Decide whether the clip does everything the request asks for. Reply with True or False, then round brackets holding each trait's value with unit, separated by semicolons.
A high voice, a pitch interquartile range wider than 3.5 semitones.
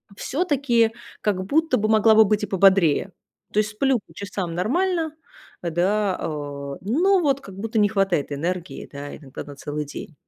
True (205 Hz; 5.4 semitones)